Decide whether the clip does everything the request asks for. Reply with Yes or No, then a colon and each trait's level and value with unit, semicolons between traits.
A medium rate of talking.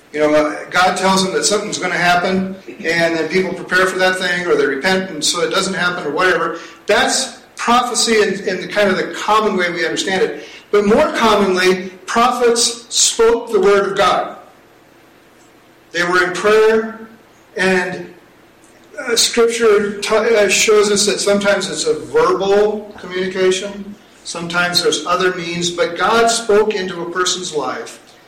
Yes: average, 160 wpm